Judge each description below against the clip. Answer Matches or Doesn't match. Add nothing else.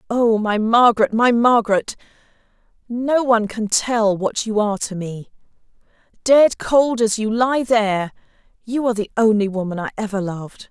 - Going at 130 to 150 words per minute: Matches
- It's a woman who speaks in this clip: Matches